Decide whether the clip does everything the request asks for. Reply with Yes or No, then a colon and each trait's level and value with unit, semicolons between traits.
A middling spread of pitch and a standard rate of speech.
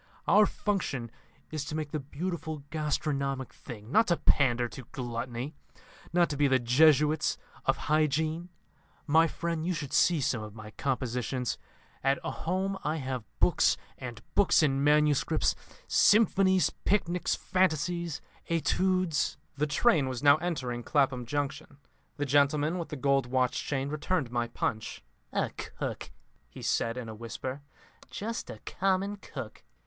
Yes: average, 4.5 semitones; average, 145 wpm